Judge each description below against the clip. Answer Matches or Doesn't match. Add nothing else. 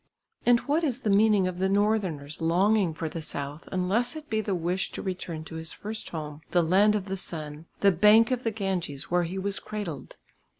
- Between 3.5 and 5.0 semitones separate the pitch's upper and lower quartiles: Matches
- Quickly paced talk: Matches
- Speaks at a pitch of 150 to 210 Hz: Matches